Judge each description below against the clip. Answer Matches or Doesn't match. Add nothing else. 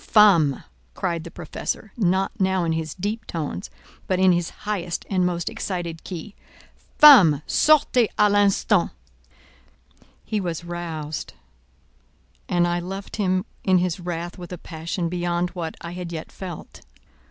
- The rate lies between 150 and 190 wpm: Doesn't match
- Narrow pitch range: Matches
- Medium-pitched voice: Matches